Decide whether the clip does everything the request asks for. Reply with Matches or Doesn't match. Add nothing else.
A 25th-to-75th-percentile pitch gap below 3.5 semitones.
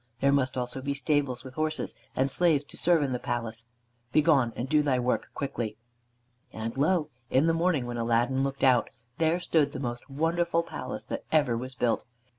Doesn't match